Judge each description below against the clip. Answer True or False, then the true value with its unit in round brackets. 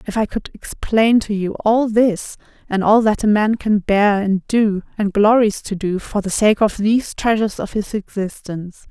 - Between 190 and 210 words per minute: True (200 wpm)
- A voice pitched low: False (210 Hz)